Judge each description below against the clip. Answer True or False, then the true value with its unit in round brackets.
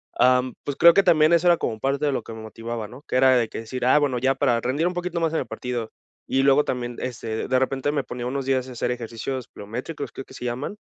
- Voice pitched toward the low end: True (130 Hz)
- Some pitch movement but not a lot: True (3.1 semitones)